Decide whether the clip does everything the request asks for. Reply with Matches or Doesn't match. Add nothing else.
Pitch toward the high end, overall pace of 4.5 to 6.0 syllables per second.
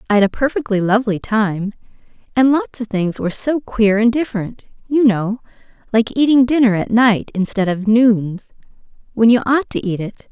Matches